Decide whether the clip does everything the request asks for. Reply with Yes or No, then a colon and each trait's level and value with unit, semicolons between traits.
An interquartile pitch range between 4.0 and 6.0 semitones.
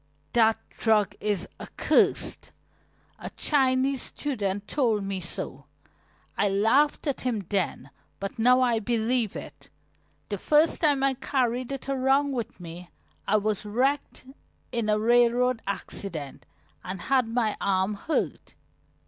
Yes: average, 4.3 semitones